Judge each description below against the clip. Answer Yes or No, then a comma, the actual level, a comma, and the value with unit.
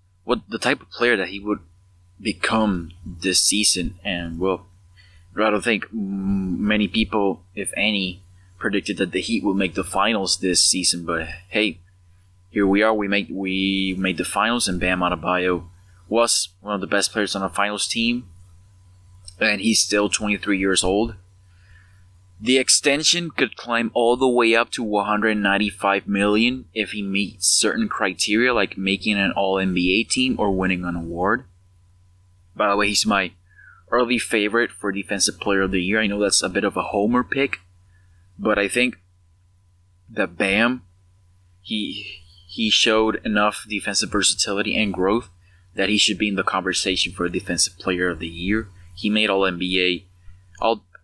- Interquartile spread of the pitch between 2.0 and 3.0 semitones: Yes, narrow, 2.6 semitones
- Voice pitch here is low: Yes, very low, 95 Hz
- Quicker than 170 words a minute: No, average, 160 wpm